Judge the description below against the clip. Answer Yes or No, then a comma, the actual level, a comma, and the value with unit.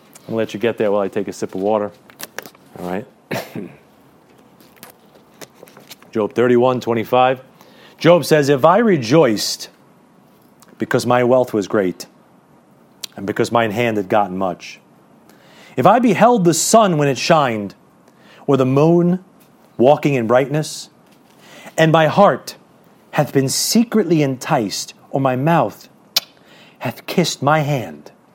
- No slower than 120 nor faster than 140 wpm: Yes, slow, 135 wpm